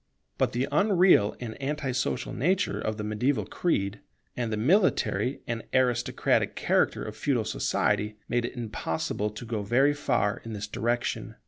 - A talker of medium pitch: No, low, 120 Hz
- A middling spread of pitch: Yes, average, 4.5 semitones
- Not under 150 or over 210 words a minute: Yes, average, 155 wpm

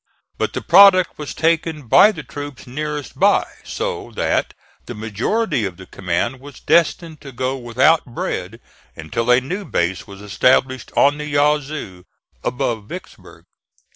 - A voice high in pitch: No, low, 135 Hz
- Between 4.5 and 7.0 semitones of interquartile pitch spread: Yes, average, 4.8 semitones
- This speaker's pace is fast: No, average, 145 wpm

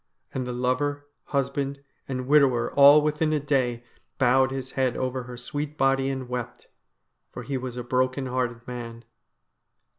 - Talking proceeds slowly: No, average, 155 wpm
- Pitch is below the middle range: Yes, low, 130 Hz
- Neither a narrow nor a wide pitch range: No, narrow, 2.0 semitones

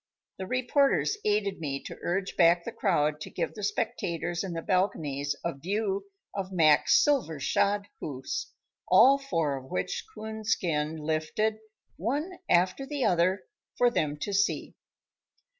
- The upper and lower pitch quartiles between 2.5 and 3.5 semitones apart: No, wide, 5.4 semitones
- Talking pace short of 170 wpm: Yes, average, 140 wpm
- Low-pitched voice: No, medium, 185 Hz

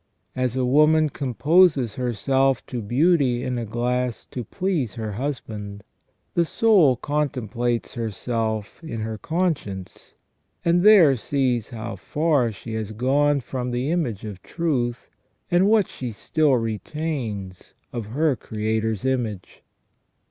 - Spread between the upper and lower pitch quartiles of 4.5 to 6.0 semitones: Yes, average, 5.2 semitones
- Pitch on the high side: No, low, 125 Hz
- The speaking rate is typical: No, slow, 125 wpm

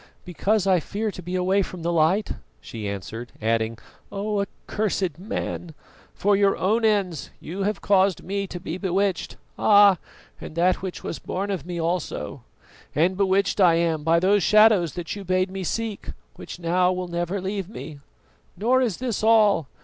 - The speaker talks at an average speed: Yes, average, 170 wpm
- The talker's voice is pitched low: No, medium, 185 Hz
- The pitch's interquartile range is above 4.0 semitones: No, average, 2.9 semitones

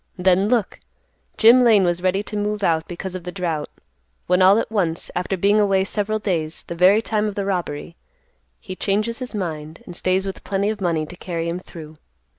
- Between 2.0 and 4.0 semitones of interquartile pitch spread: Yes, average, 3.1 semitones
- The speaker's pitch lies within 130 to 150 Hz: No, high, 190 Hz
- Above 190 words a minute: Yes, fast, 205 wpm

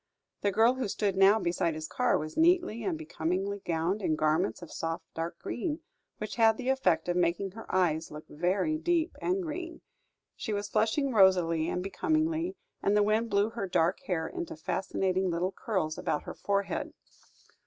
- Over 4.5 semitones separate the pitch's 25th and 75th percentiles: Yes, wide, 5.5 semitones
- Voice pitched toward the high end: Yes, high, 195 Hz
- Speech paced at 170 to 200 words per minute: Yes, average, 175 wpm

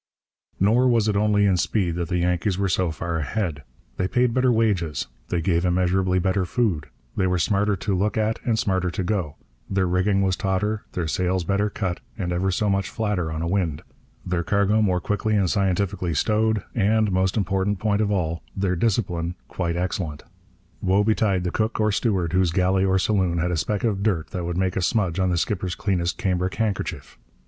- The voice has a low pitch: Yes, very low, 95 Hz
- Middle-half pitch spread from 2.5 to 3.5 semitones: Yes, average, 2.8 semitones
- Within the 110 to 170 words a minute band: No, average, 200 wpm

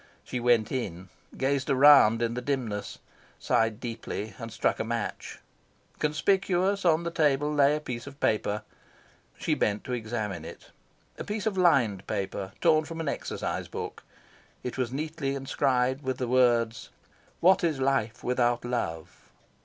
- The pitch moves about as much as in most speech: Yes, average, 4.6 semitones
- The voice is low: Yes, low, 125 Hz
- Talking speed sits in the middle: Yes, average, 155 wpm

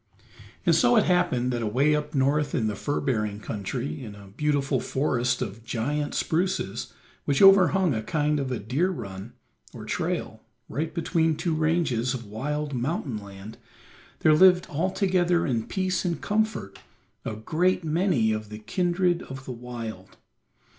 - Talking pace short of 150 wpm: No, average, 155 wpm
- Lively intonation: Yes, wide, 7.1 semitones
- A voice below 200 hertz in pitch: Yes, medium, 140 Hz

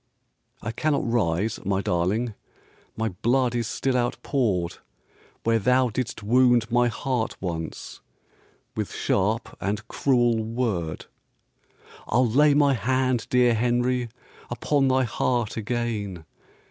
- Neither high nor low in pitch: No, low, 120 Hz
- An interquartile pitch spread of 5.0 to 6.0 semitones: No, average, 2.9 semitones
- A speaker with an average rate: No, slow, 115 wpm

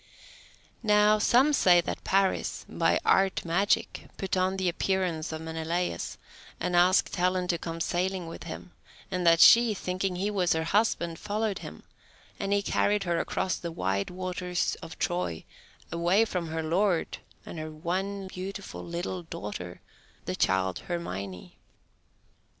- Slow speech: No, average, 145 wpm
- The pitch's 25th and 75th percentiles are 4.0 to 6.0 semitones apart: No, average, 2.8 semitones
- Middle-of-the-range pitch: Yes, medium, 180 Hz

